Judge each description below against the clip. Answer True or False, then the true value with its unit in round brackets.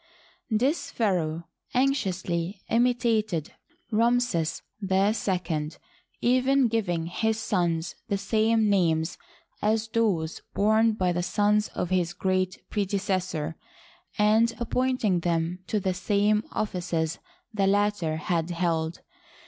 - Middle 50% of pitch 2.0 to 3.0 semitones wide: False (4.2 semitones)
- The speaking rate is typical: False (105 wpm)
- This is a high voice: True (195 Hz)